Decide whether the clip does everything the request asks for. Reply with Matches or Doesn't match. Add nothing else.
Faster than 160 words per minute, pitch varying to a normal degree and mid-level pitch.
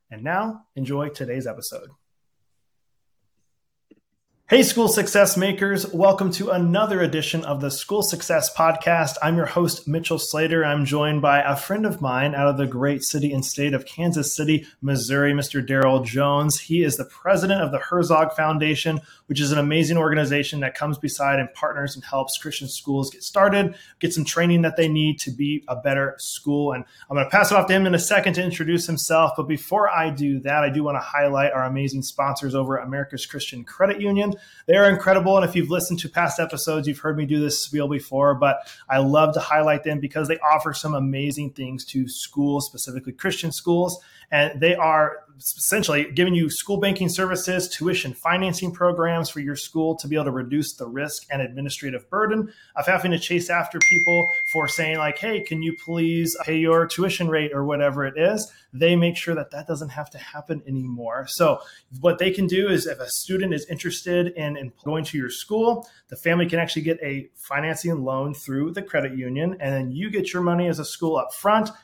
Matches